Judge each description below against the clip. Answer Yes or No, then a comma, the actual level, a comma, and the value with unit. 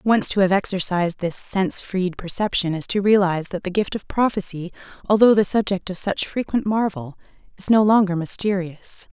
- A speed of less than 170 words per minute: No, average, 175 wpm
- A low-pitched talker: No, high, 190 Hz